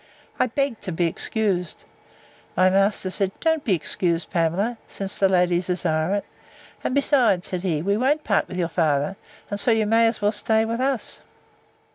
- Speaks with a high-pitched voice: Yes, high, 195 Hz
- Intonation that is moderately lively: Yes, average, 4.1 semitones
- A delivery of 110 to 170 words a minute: No, average, 180 wpm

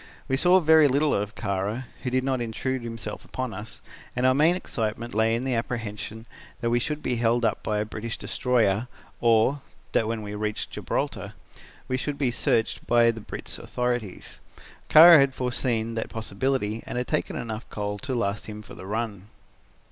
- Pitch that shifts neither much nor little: Yes, average, 3.1 semitones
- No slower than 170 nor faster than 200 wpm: Yes, average, 185 wpm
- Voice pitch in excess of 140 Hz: No, low, 115 Hz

